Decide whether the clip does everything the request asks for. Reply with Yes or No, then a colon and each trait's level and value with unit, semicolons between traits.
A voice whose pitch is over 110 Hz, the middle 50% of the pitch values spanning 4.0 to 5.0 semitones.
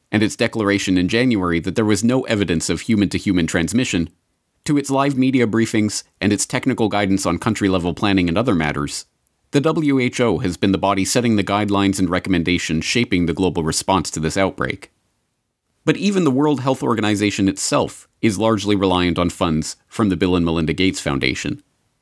No: low, 100 Hz; average, 4.7 semitones